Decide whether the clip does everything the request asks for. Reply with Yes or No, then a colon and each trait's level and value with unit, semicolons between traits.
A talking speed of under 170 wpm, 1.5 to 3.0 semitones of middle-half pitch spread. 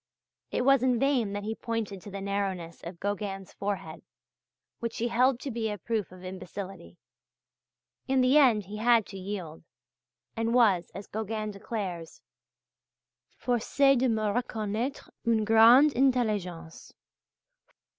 No: slow, 135 wpm; average, 3.7 semitones